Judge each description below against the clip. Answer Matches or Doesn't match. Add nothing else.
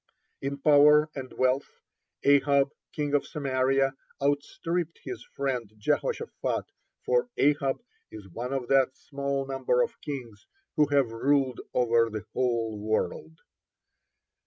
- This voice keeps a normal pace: Doesn't match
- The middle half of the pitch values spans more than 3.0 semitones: Doesn't match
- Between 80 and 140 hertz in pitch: Matches